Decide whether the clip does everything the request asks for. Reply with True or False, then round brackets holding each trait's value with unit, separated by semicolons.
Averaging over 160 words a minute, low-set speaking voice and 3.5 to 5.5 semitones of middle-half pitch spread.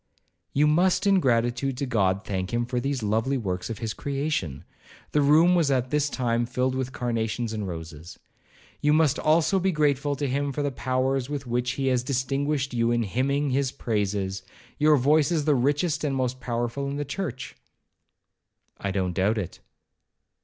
True (170 wpm; 130 Hz; 3.8 semitones)